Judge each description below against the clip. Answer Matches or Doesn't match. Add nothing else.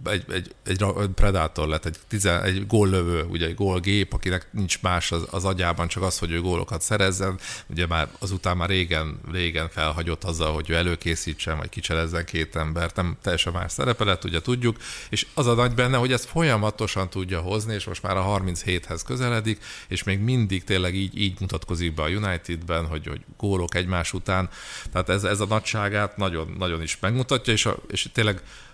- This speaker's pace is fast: Matches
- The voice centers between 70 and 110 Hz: Matches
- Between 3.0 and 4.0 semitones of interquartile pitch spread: Matches